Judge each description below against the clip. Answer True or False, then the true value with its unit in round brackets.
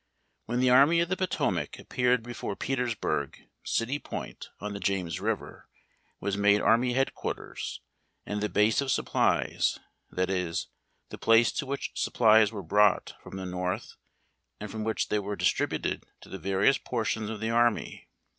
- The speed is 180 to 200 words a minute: False (165 wpm)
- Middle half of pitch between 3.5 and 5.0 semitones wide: True (3.8 semitones)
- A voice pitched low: True (110 Hz)